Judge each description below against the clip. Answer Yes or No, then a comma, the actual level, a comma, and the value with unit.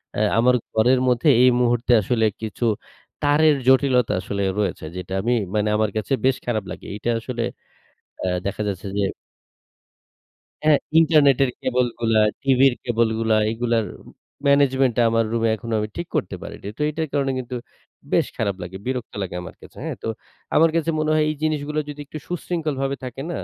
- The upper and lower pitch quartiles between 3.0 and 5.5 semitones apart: Yes, average, 4.2 semitones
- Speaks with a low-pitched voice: Yes, low, 125 Hz